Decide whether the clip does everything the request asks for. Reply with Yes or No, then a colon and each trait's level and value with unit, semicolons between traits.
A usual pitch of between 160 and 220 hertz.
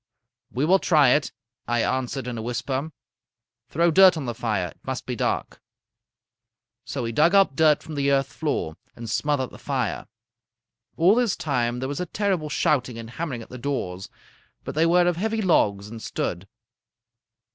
No: medium, 140 Hz